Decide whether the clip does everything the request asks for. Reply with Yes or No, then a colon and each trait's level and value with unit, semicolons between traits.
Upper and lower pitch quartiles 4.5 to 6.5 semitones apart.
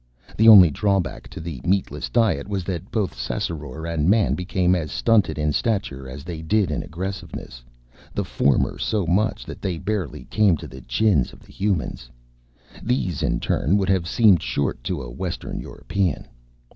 Yes: average, 5.2 semitones